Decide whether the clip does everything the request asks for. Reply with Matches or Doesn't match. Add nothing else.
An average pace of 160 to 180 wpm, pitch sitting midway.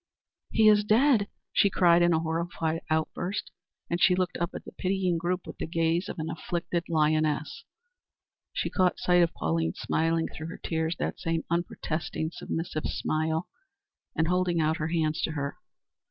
Matches